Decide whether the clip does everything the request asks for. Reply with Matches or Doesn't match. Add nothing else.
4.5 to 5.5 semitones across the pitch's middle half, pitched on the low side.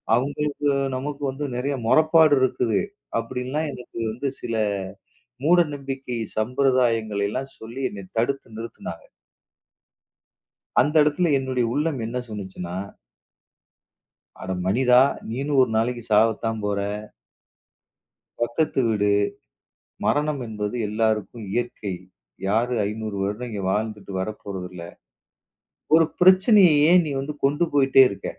Matches